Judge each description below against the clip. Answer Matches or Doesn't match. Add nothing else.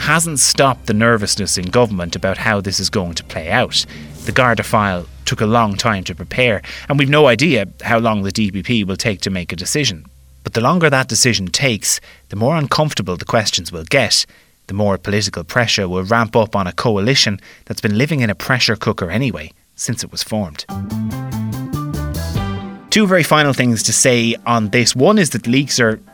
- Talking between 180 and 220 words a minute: Matches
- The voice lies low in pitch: Matches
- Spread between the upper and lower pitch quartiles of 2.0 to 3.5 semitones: Doesn't match